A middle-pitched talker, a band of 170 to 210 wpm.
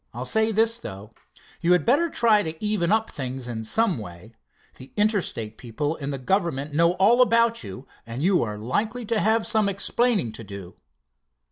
Yes: medium, 170 Hz; average, 180 wpm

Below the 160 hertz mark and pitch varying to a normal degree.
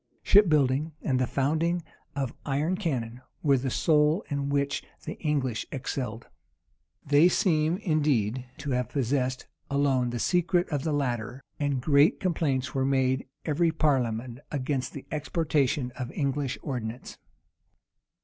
Yes: medium, 140 Hz; average, 3.2 semitones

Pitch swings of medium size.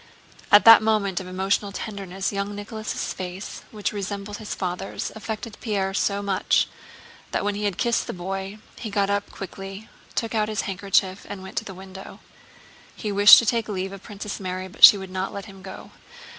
No: narrow, 1.6 semitones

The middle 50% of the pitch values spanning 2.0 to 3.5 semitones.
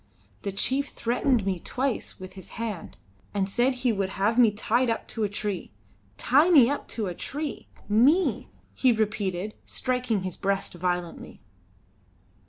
No: average, 4.6 semitones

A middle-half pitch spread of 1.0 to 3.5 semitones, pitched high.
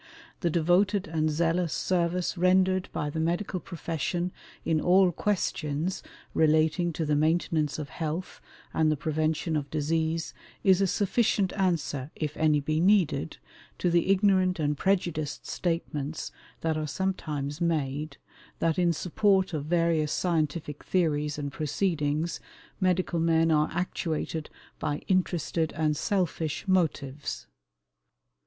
No: average, 3.0 semitones; medium, 165 Hz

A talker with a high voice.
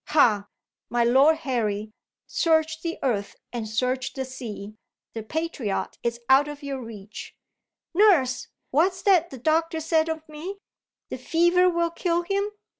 Yes: very high, 295 Hz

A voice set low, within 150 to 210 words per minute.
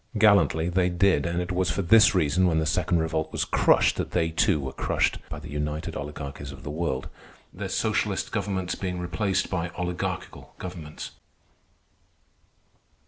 Yes: very low, 85 Hz; average, 160 wpm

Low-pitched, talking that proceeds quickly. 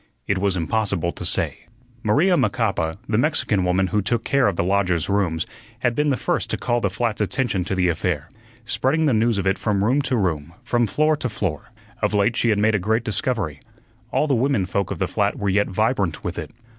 Yes: low, 105 Hz; fast, 220 wpm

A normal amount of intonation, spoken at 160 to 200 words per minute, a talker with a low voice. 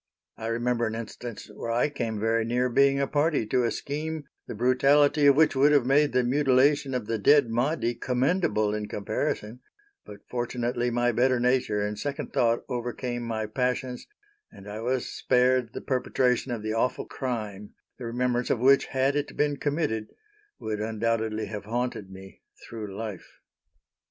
Yes: average, 3.0 semitones; average, 165 wpm; low, 120 Hz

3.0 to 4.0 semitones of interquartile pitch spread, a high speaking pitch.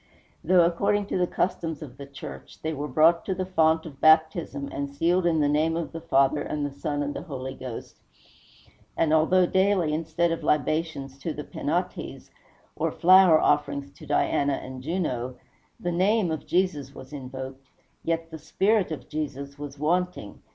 No: average, 3.4 semitones; medium, 155 Hz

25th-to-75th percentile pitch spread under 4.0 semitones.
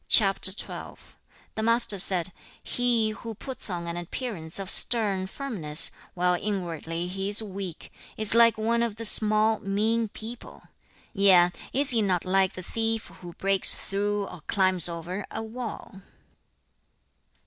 Yes: average, 3.4 semitones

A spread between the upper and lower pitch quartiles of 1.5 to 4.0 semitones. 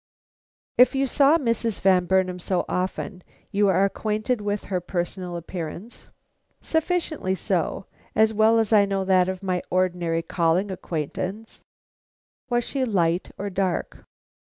Yes: average, 3.4 semitones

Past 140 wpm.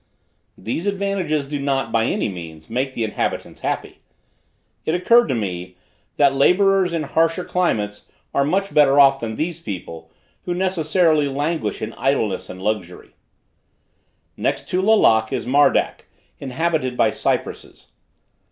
No: slow, 135 wpm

